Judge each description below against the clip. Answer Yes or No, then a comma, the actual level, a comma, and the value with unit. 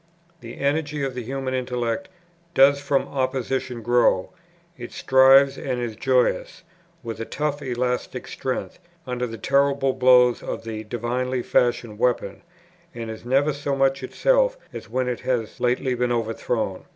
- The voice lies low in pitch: Yes, low, 125 Hz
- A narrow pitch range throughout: Yes, narrow, 2.2 semitones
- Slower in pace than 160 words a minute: Yes, average, 150 wpm